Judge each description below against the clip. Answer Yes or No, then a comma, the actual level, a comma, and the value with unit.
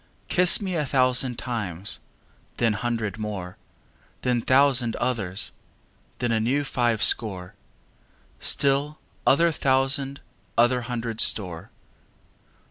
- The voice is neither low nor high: No, low, 120 Hz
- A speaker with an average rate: No, slow, 105 wpm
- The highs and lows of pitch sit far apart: No, average, 3.8 semitones